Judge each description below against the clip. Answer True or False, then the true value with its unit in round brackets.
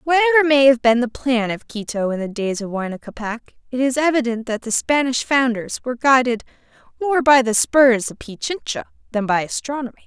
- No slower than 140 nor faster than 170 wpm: False (190 wpm)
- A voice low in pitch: False (250 Hz)